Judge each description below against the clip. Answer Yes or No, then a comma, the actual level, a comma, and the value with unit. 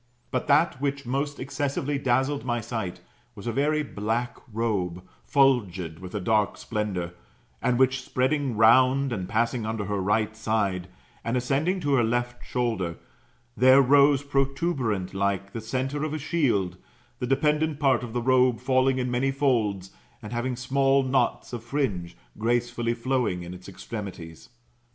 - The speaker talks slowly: No, average, 155 wpm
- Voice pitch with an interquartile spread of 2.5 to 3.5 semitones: No, average, 4.3 semitones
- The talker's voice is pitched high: No, low, 120 Hz